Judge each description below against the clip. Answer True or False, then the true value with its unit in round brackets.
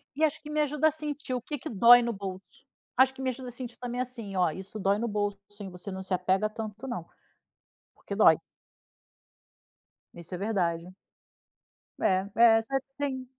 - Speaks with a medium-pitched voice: False (225 Hz)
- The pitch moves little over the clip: False (5.2 semitones)